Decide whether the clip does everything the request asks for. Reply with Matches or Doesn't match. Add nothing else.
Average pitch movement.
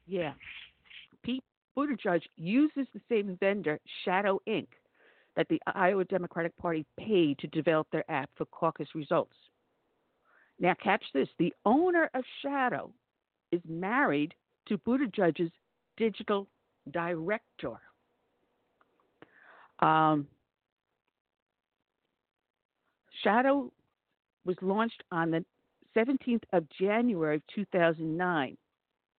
Doesn't match